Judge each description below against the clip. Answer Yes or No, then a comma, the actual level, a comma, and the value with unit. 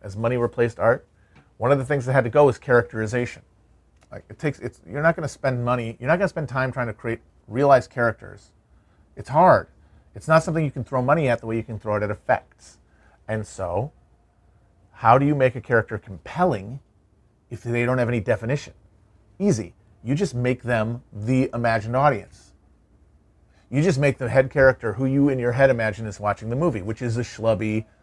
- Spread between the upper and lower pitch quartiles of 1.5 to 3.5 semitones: No, average, 4.0 semitones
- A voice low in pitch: Yes, low, 120 Hz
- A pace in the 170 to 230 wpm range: Yes, fast, 205 wpm